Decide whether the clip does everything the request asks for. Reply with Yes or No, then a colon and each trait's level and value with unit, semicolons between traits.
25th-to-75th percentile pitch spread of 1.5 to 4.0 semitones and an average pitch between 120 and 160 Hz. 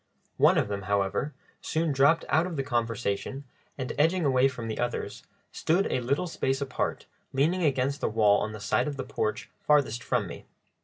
No: average, 4.6 semitones; low, 135 Hz